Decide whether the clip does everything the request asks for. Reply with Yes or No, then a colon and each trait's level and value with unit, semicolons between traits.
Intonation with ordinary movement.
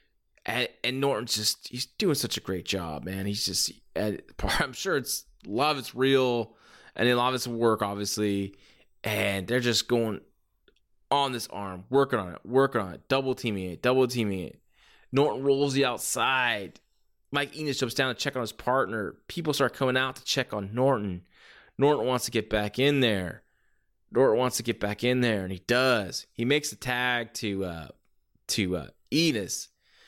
Yes: average, 4.3 semitones